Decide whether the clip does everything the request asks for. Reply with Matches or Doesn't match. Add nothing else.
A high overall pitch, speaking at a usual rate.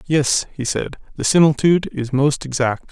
Doesn't match